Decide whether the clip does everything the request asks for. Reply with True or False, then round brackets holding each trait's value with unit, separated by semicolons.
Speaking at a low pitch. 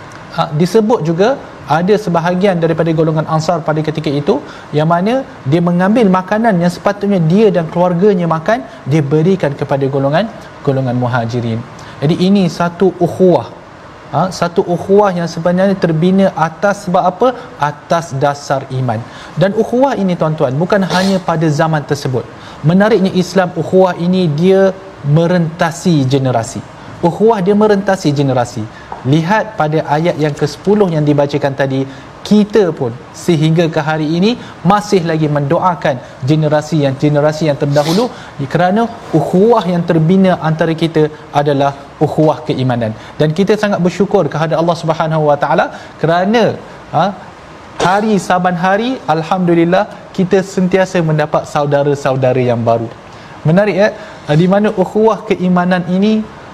False (170 Hz)